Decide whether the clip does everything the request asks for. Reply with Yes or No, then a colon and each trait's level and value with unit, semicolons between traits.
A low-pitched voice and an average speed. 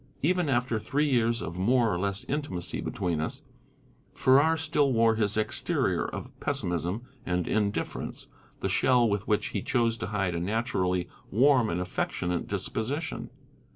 Yes: low, 110 Hz; average, 150 wpm